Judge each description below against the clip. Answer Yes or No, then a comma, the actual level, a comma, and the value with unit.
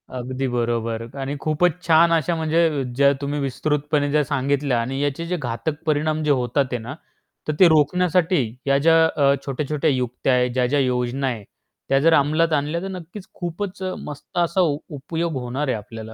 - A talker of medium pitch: Yes, medium, 145 Hz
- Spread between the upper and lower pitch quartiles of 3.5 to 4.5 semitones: Yes, average, 3.8 semitones